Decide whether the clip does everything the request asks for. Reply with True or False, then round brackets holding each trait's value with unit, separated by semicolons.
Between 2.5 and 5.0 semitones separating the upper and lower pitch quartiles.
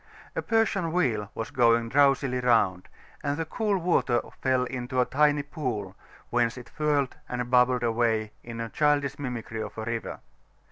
True (3.7 semitones)